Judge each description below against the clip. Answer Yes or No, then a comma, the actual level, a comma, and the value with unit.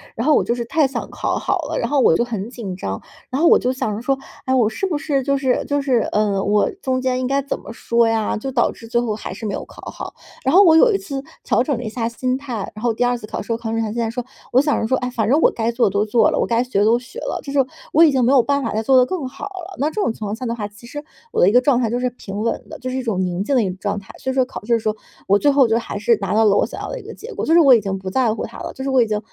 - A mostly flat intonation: No, average, 3.6 semitones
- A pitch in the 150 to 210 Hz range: No, high, 245 Hz